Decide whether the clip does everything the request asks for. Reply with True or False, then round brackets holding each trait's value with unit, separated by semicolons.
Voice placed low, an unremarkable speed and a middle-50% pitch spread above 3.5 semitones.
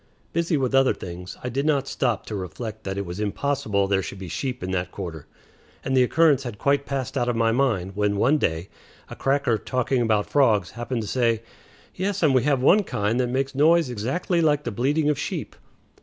False (125 Hz; 215 wpm; 5.3 semitones)